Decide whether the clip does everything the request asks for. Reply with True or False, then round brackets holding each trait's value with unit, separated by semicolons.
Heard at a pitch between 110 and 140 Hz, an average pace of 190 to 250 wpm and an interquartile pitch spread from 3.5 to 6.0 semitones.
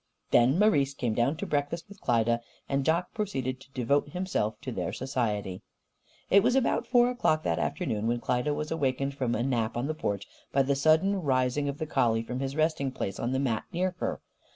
True (135 Hz; 205 wpm; 4.6 semitones)